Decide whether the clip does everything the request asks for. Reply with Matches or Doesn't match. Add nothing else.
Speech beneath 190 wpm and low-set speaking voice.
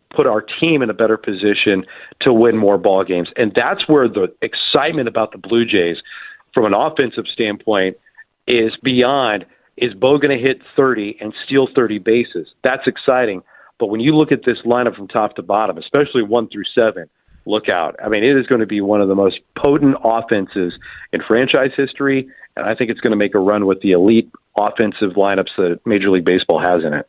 Doesn't match